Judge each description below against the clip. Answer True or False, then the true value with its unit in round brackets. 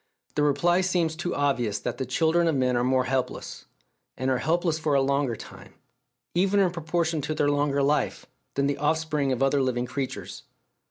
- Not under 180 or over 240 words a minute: True (195 wpm)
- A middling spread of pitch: True (3.4 semitones)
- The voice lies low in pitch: False (145 Hz)